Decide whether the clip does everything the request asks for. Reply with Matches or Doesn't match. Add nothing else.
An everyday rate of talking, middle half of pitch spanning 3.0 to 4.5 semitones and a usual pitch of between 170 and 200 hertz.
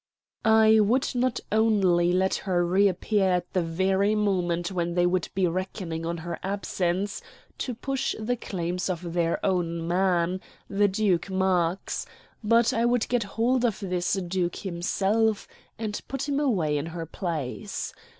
Matches